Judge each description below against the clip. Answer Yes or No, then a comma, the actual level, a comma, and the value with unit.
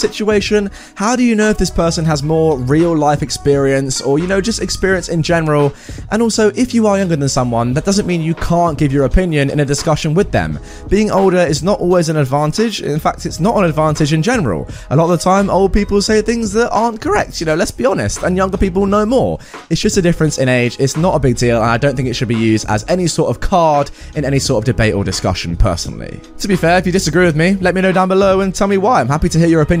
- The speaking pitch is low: No, medium, 170 Hz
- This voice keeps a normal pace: No, fast, 270 wpm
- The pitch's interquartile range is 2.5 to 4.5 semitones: No, wide, 5.5 semitones